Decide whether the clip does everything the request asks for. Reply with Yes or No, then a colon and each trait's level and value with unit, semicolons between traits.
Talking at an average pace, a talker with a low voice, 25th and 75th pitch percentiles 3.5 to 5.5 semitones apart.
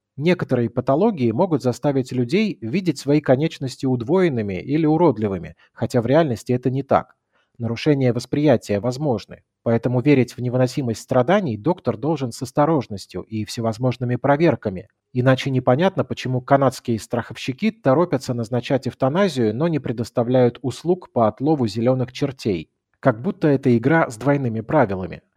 Yes: average, 130 wpm; low, 130 Hz; average, 3.9 semitones